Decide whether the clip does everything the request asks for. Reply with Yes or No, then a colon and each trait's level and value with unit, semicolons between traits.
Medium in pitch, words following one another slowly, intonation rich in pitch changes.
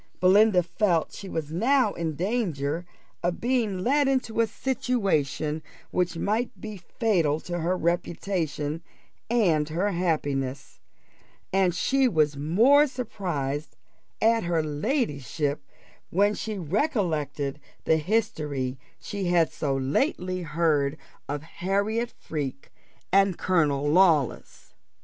Yes: medium, 175 Hz; slow, 115 wpm; wide, 5.9 semitones